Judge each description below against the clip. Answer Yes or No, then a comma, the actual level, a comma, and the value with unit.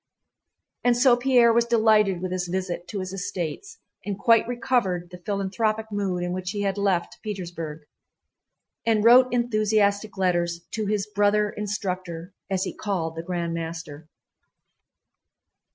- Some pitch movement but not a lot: Yes, average, 3.4 semitones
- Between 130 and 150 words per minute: Yes, average, 140 wpm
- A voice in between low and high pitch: No, high, 200 Hz